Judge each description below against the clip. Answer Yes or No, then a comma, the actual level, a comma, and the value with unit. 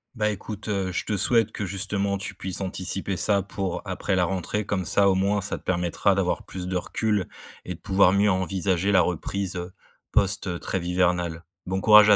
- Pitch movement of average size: No, narrow, 1.9 semitones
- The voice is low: Yes, very low, 95 Hz